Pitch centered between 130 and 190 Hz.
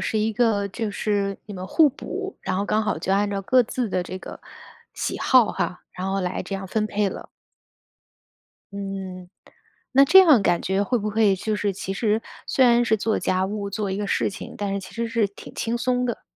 No: high, 205 Hz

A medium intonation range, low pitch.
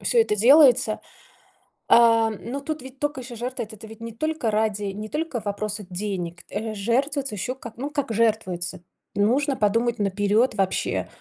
No: average, 4.1 semitones; high, 225 Hz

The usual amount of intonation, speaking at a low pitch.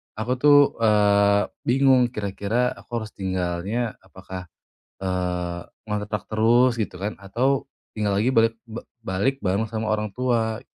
Yes: average, 3.3 semitones; low, 110 Hz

